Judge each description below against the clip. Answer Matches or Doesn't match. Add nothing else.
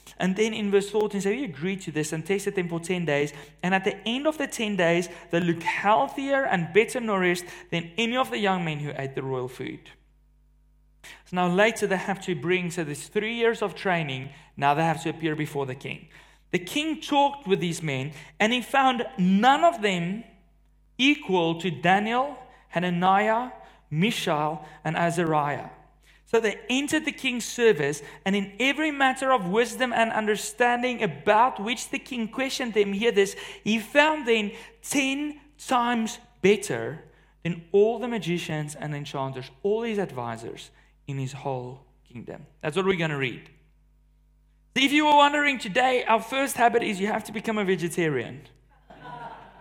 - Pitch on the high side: Matches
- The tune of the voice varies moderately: Doesn't match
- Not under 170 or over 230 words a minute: Matches